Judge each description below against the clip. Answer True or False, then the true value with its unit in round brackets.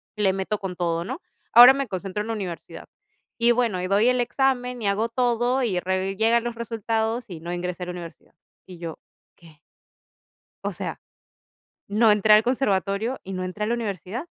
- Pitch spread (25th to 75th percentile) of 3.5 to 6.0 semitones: True (4.3 semitones)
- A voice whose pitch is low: False (210 Hz)